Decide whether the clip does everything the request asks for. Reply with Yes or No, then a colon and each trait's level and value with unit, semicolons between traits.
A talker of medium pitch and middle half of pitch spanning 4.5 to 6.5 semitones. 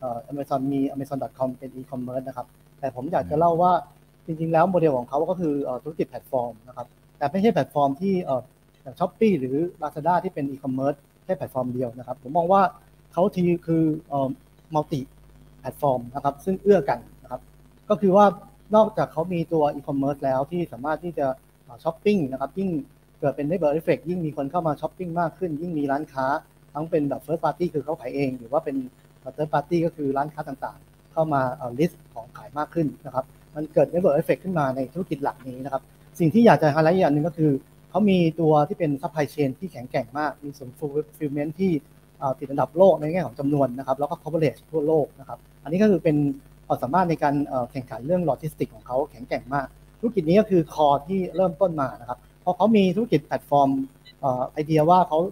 No: medium, 150 Hz; average, 3.5 semitones